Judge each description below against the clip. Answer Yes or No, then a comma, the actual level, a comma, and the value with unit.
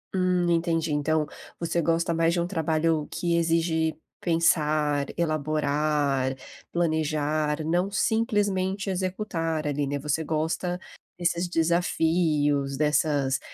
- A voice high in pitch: No, medium, 160 Hz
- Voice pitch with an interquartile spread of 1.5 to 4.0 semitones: Yes, narrow, 2.4 semitones